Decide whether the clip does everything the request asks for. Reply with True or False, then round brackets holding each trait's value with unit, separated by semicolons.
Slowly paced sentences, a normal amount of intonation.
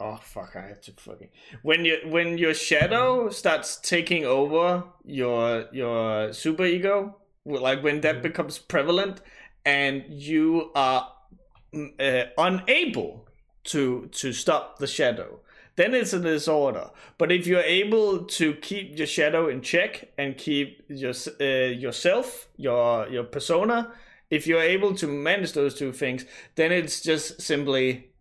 False (145 wpm; 4.6 semitones)